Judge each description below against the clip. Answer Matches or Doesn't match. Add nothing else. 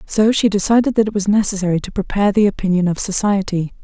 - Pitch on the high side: Matches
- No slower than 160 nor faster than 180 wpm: Doesn't match